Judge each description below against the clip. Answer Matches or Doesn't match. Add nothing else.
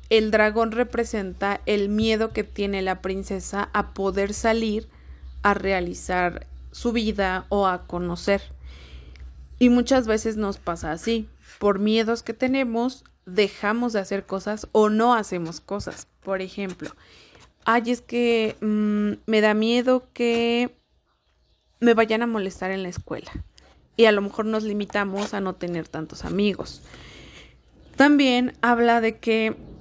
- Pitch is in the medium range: Doesn't match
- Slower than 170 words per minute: Matches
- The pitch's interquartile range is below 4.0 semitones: Matches